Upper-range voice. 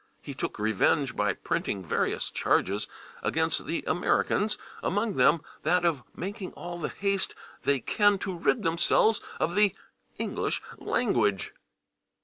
No: medium, 170 Hz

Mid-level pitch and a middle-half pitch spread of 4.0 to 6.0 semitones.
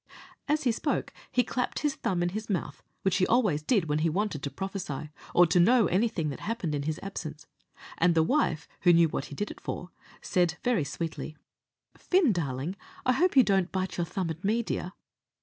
Yes: medium, 180 Hz; average, 5.2 semitones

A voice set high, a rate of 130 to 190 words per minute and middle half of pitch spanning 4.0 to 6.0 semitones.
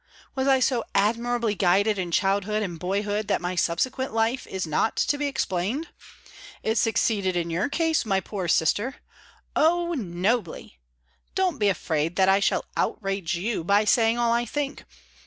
Yes: high, 210 Hz; average, 160 wpm; average, 4.5 semitones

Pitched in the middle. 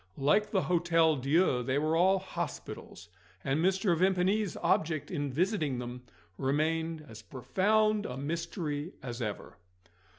Yes: medium, 160 Hz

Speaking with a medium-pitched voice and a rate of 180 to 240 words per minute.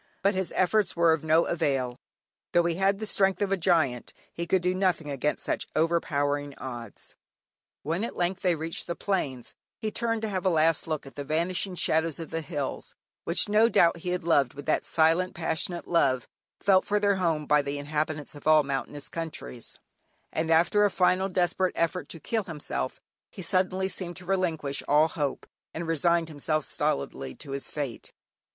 Yes: medium, 165 Hz; average, 185 wpm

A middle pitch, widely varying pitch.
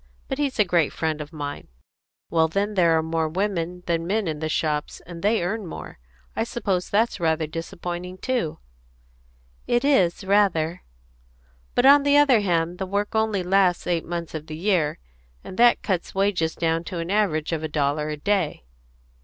No: medium, 175 Hz; average, 4.2 semitones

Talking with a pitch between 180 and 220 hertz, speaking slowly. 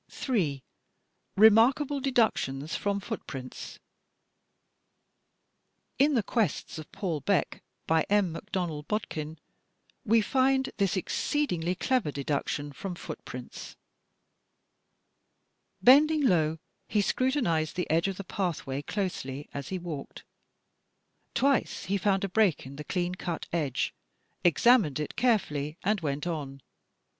Yes: medium, 185 Hz; slow, 120 wpm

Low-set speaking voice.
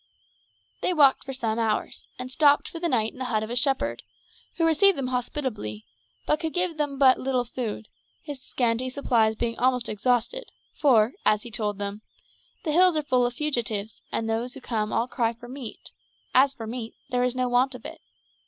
No: very high, 250 Hz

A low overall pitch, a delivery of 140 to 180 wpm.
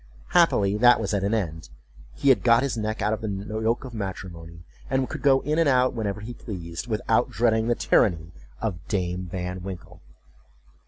No: low, 105 Hz; average, 190 wpm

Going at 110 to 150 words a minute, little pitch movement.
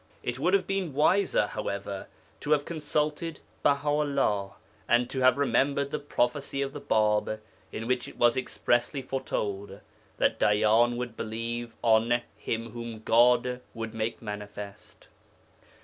No: average, 140 wpm; average, 4.3 semitones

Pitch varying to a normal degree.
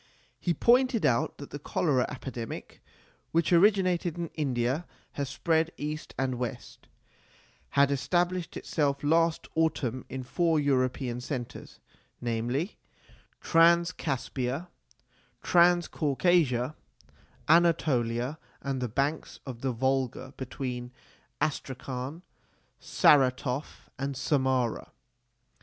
Yes: average, 4.5 semitones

